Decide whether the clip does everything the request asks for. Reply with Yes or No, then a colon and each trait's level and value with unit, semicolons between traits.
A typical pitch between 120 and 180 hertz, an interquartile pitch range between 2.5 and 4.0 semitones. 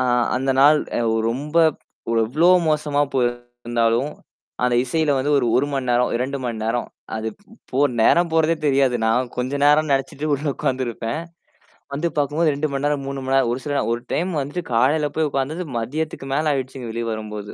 Yes: low, 135 Hz; average, 3.5 semitones